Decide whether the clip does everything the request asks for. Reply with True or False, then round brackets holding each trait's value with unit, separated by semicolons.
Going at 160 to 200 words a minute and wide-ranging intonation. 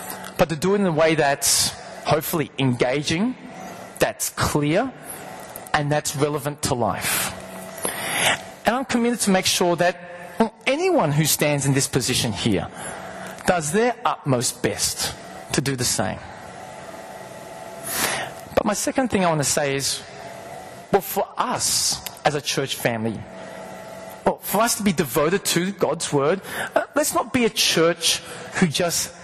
False (145 wpm; 6.4 semitones)